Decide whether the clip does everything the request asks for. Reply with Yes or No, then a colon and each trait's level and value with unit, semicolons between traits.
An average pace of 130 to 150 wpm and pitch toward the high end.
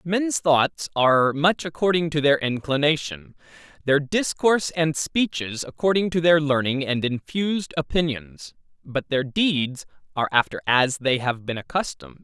No: average, 140 wpm; medium, 145 Hz